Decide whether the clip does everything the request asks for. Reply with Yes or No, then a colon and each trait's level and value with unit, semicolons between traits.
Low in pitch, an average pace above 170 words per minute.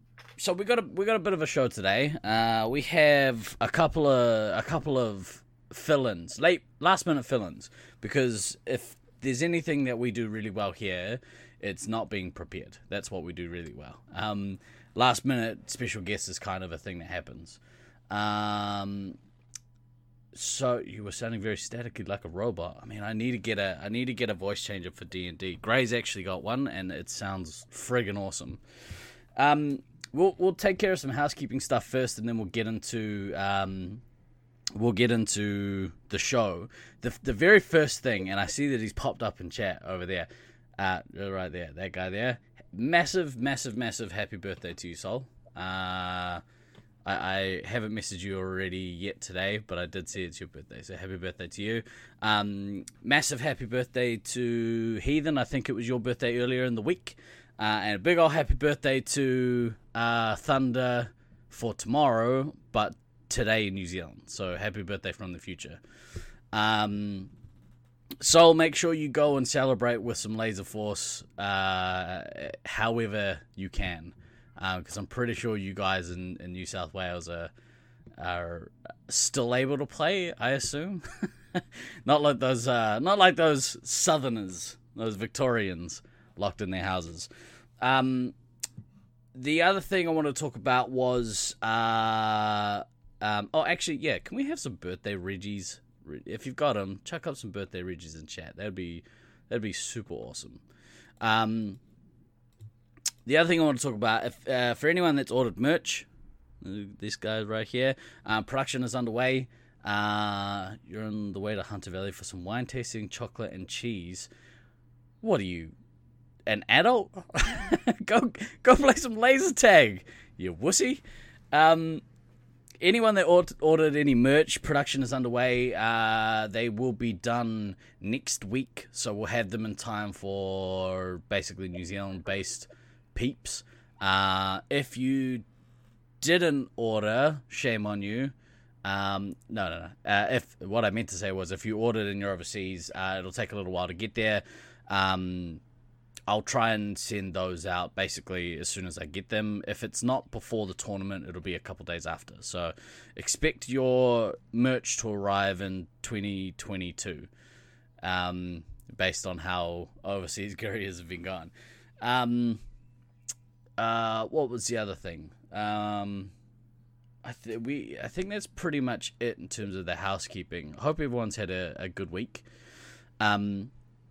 No: low, 115 Hz; average, 165 wpm